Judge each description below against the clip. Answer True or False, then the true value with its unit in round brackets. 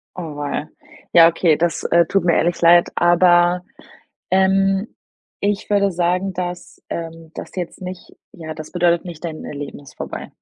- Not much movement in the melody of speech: True (1.8 semitones)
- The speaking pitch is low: False (175 Hz)